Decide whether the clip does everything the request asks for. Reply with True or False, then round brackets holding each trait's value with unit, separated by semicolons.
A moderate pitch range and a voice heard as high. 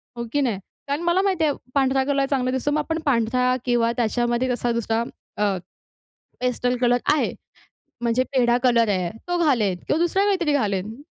True (3.7 semitones; 250 Hz)